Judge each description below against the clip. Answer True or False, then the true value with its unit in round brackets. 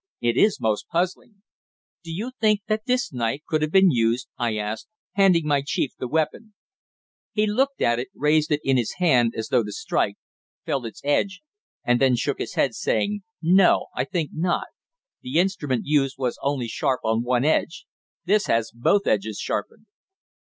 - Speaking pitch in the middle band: True (145 Hz)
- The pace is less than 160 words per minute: False (180 wpm)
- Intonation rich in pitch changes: True (7.7 semitones)